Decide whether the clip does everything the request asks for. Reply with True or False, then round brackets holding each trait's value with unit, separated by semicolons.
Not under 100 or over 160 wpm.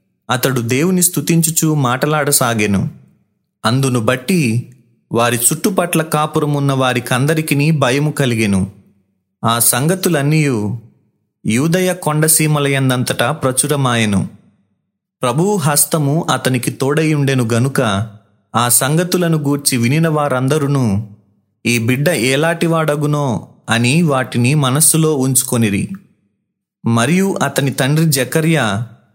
False (80 wpm)